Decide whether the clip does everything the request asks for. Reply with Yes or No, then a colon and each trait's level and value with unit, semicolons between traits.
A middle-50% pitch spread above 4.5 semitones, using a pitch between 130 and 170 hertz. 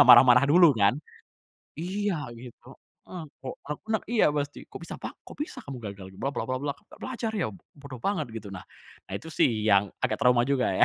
Yes: wide, 5.4 semitones; medium, 140 Hz